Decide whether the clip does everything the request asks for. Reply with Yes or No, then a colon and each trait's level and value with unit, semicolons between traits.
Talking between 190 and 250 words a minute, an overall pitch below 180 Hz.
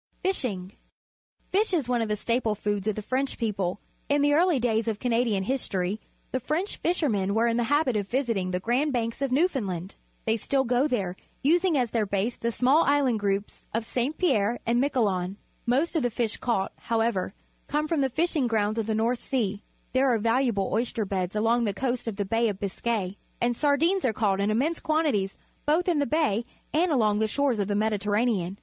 No: average, 200 wpm; high, 235 Hz